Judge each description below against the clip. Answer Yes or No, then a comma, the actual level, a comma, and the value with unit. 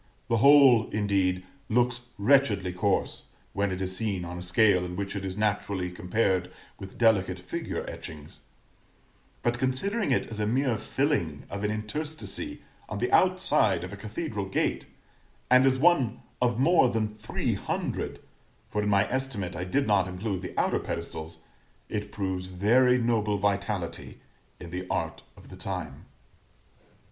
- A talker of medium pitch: No, low, 105 Hz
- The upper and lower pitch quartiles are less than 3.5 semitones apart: No, average, 4.8 semitones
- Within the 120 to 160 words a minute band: Yes, average, 155 wpm